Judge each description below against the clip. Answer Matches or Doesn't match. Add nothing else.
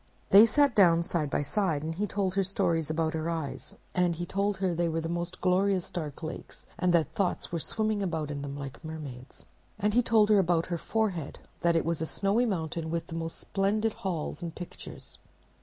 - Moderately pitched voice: Matches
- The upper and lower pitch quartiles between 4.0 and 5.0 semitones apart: Doesn't match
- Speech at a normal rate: Doesn't match